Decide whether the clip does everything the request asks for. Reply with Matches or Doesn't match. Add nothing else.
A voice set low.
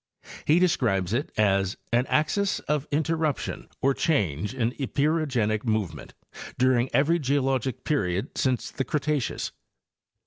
Matches